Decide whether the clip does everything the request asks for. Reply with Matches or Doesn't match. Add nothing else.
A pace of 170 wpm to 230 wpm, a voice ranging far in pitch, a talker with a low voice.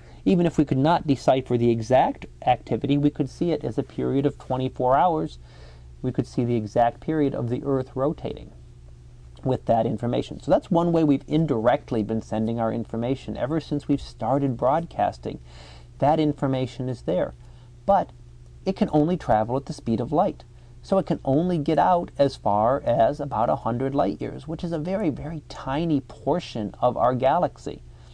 Doesn't match